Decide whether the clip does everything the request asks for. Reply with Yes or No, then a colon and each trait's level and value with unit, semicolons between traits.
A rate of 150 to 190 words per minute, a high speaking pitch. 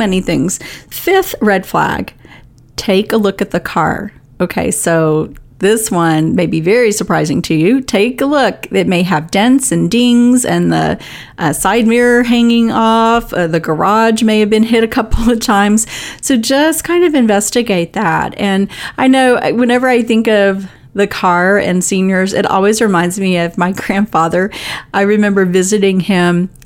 Yes: average, 170 wpm; high, 205 Hz